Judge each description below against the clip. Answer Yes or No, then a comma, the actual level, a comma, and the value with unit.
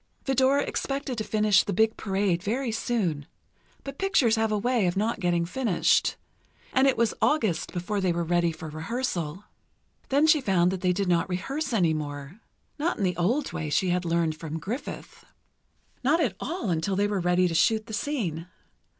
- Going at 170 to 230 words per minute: Yes, average, 180 wpm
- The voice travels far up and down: Yes, wide, 6.1 semitones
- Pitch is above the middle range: Yes, high, 200 Hz